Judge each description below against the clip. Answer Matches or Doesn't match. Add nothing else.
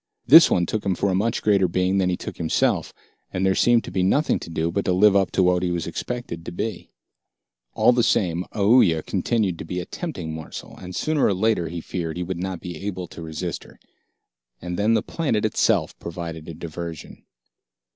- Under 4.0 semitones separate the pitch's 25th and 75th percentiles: Matches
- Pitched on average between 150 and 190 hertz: Doesn't match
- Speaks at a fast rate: Matches